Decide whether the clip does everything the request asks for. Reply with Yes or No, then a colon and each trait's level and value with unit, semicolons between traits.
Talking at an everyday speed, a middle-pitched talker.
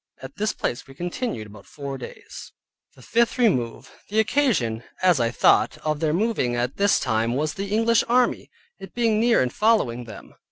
Yes: average, 185 wpm; medium, 155 Hz